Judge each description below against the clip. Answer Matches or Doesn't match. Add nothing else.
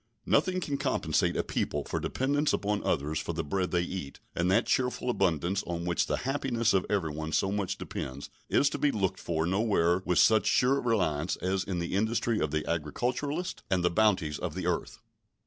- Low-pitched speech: Matches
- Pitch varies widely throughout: Matches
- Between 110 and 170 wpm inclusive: Doesn't match